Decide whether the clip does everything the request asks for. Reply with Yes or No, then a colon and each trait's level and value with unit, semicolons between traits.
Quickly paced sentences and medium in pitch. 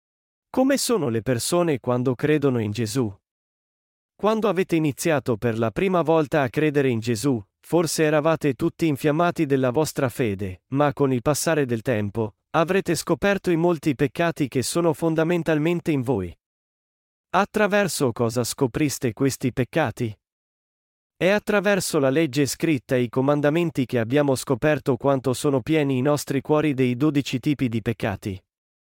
No: average, 145 wpm; medium, 145 Hz